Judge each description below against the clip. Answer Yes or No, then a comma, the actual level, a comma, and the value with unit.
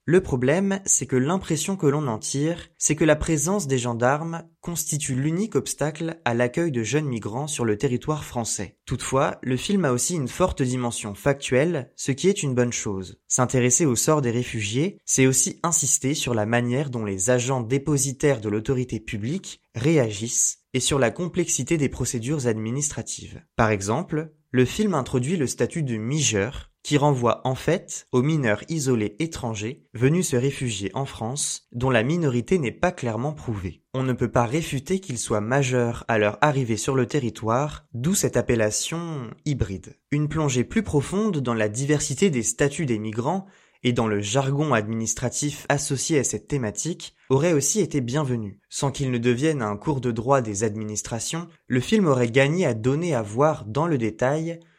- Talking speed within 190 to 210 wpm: No, average, 175 wpm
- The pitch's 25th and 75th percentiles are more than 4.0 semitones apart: Yes, average, 4.6 semitones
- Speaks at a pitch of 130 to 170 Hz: Yes, low, 135 Hz